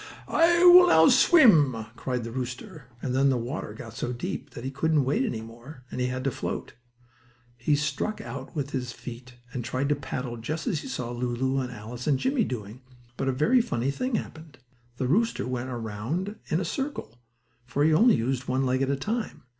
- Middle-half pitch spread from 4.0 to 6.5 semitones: Yes, average, 4.5 semitones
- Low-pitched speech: Yes, low, 130 Hz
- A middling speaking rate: No, fast, 215 wpm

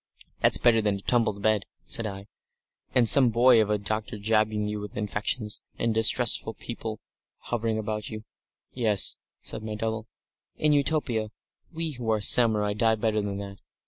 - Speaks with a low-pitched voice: Yes, low, 110 Hz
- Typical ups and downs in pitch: No, narrow, 1.8 semitones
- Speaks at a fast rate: No, average, 165 wpm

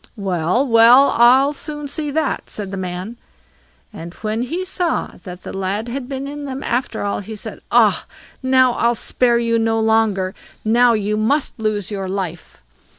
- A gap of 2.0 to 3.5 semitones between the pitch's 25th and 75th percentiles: No, average, 4.7 semitones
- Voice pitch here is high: Yes, high, 230 Hz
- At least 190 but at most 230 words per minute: No, average, 170 wpm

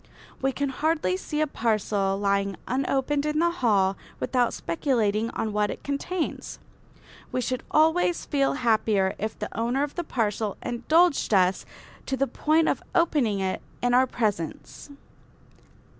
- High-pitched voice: Yes, high, 245 Hz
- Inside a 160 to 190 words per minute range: No, average, 145 wpm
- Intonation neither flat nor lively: No, wide, 6.0 semitones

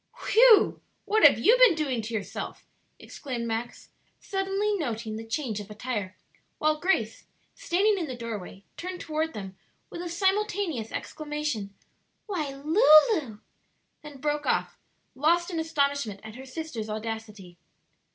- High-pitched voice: Yes, very high, 290 Hz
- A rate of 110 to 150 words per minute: Yes, average, 140 wpm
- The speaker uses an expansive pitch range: Yes, wide, 7.6 semitones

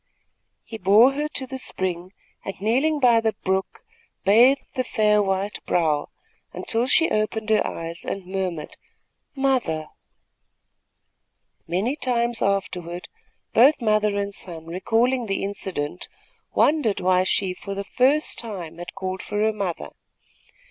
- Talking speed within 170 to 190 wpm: No, slow, 135 wpm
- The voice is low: No, high, 205 Hz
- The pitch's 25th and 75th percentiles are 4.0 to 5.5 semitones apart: Yes, average, 4.4 semitones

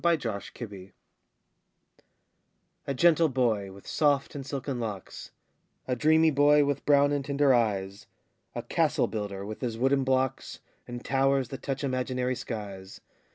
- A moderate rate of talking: Yes, average, 145 wpm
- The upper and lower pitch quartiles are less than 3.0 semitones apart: No, average, 4.6 semitones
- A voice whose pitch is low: Yes, low, 130 Hz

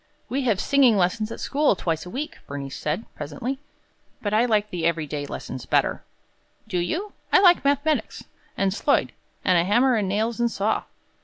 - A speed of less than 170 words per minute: No, average, 180 wpm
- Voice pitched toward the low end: No, high, 215 Hz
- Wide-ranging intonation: Yes, wide, 6.7 semitones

